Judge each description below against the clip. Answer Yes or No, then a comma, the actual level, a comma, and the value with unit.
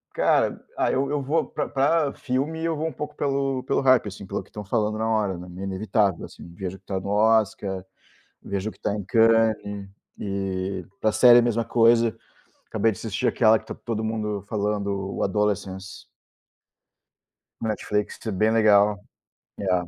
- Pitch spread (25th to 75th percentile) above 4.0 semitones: No, average, 3.0 semitones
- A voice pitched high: No, low, 105 Hz